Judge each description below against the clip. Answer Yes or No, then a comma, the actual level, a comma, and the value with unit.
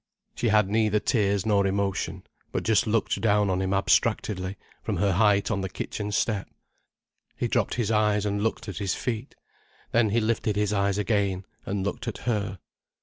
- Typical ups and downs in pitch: No, narrow, 1.6 semitones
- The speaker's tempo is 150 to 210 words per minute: Yes, average, 180 wpm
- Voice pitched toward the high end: No, low, 105 Hz